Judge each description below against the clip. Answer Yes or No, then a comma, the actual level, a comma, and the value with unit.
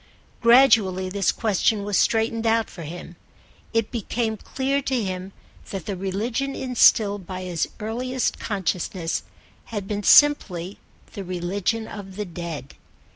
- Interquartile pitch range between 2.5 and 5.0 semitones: Yes, average, 3.7 semitones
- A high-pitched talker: Yes, high, 205 Hz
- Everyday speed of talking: No, slow, 130 wpm